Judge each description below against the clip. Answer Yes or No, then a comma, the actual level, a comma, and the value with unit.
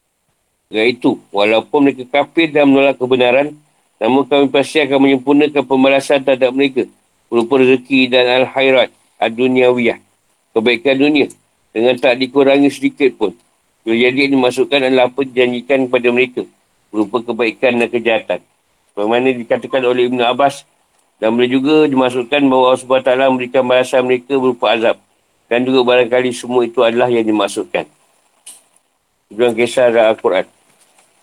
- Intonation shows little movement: Yes, narrow, 2.0 semitones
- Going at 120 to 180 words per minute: Yes, average, 130 wpm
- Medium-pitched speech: No, low, 130 Hz